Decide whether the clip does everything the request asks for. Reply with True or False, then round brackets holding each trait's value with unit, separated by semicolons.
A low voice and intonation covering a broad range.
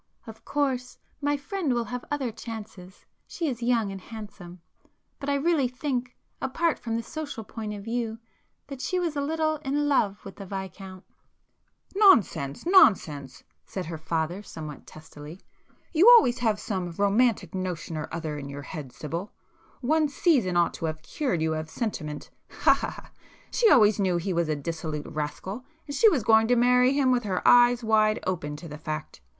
False (215 Hz; 7.6 semitones)